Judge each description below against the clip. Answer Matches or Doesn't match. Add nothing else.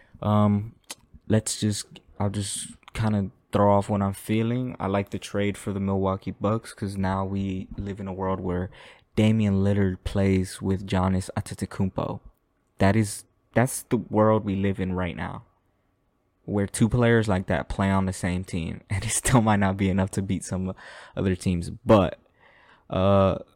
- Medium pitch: Doesn't match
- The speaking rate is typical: Matches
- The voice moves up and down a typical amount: Doesn't match